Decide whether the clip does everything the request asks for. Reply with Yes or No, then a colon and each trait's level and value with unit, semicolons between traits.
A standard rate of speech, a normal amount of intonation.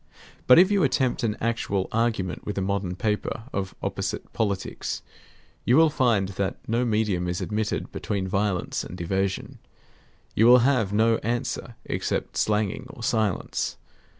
Yes: average, 150 wpm; average, 3.5 semitones